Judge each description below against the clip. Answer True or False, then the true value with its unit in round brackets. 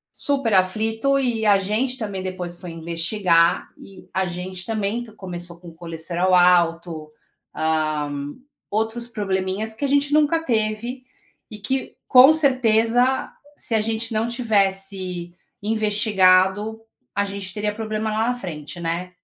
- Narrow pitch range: False (3.8 semitones)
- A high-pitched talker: True (205 Hz)